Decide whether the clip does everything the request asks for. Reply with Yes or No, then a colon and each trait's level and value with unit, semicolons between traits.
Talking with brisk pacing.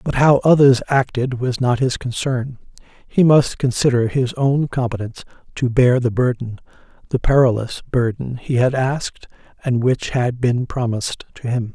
No: average, 155 wpm